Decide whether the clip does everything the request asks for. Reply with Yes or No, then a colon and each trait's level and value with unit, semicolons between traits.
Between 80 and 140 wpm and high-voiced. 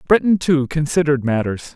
No: slow, 135 wpm; medium, 150 Hz